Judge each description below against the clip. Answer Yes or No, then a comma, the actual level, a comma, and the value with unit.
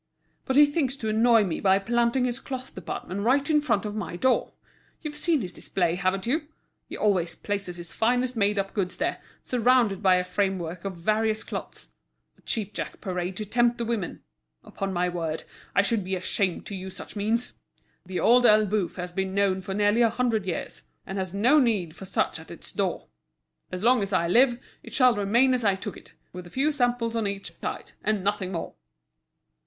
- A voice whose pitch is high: Yes, high, 205 Hz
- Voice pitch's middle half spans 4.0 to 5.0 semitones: Yes, average, 4.3 semitones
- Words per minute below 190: No, average, 200 wpm